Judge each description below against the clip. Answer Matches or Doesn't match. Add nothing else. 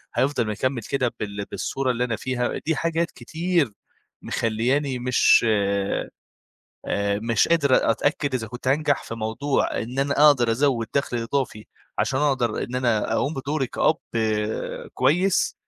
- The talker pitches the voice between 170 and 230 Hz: Doesn't match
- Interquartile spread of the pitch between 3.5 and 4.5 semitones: Matches